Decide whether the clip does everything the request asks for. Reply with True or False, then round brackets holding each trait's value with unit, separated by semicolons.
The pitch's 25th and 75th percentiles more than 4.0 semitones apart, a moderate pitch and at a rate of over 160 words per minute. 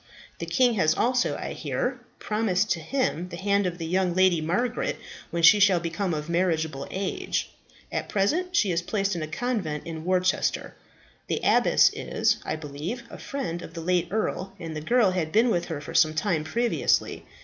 True (4.4 semitones; 180 Hz; 190 wpm)